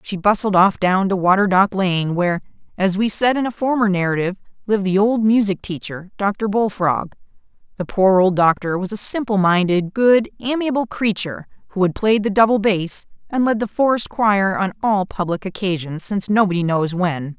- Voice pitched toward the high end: Yes, high, 195 Hz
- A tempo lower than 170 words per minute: No, average, 185 wpm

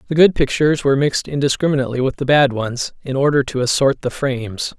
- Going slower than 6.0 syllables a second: No, 6.5 syllables/s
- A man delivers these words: Yes, male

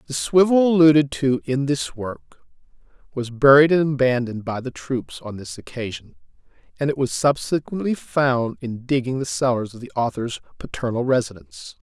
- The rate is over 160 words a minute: No, average, 155 wpm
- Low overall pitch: Yes, low, 130 Hz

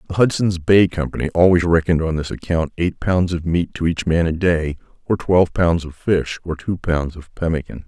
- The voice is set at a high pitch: No, very low, 85 Hz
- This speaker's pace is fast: Yes, fast, 215 wpm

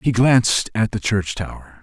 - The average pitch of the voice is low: Yes, low, 110 Hz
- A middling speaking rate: Yes, average, 195 wpm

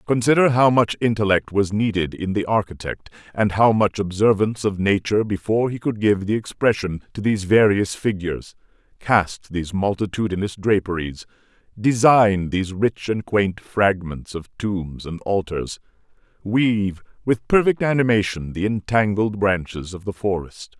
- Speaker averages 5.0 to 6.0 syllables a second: No, 4.8 syllables/s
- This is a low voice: Yes, low, 100 Hz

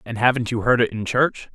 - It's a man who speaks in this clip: Yes, male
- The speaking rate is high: Yes, fast, 270 wpm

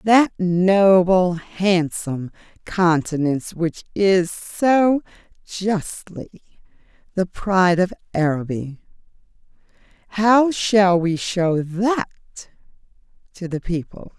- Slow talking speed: Yes, slow, 80 wpm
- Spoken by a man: No, female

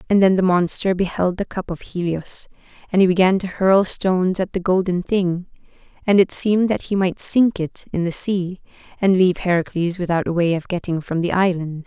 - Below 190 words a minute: No, fast, 205 wpm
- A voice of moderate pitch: Yes, medium, 180 Hz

